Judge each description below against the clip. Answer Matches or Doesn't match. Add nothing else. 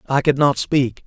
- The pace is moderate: Doesn't match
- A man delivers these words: Matches